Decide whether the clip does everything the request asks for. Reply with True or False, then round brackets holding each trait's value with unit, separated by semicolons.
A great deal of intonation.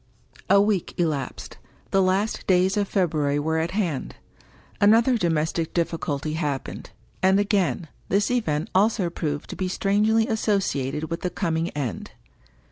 False (4.5 semitones)